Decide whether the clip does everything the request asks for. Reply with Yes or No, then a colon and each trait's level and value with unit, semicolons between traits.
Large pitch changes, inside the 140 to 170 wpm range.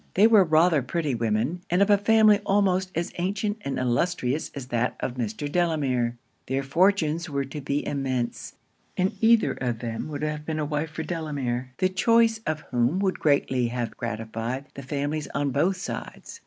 No: wide, 6.2 semitones; average, 180 wpm